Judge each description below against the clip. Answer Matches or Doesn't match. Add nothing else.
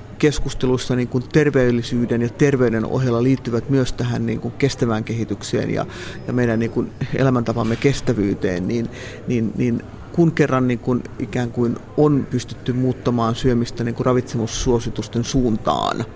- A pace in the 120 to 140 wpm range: Matches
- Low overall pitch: Matches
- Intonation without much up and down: Matches